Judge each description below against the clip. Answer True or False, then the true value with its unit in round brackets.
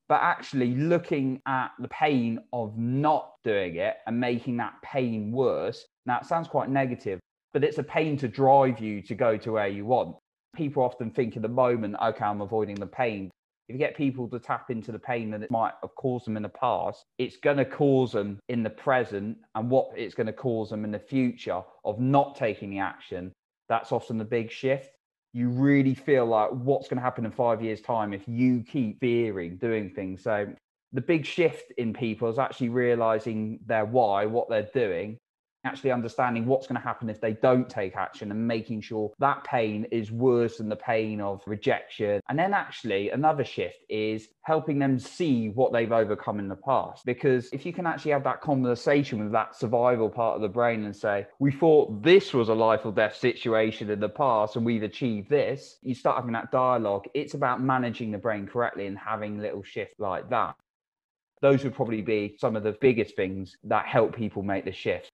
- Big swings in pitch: False (3.4 semitones)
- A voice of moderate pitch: False (120 Hz)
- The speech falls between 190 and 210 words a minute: True (205 wpm)